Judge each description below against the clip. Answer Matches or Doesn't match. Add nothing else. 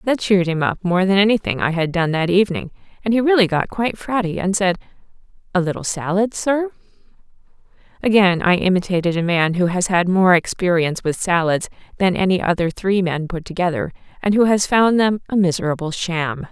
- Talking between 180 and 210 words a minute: Matches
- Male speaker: Doesn't match